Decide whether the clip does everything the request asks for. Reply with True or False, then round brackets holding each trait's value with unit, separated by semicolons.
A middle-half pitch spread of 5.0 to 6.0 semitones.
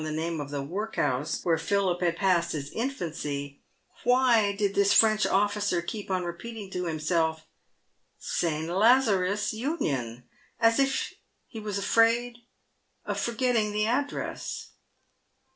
True (5.6 semitones)